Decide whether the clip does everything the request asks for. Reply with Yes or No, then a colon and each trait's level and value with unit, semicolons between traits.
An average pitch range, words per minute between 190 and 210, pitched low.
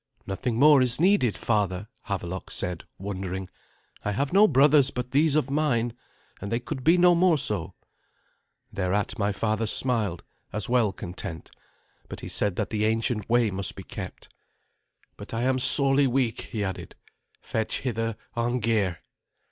No: average, 4.7 semitones; average, 155 wpm; low, 115 Hz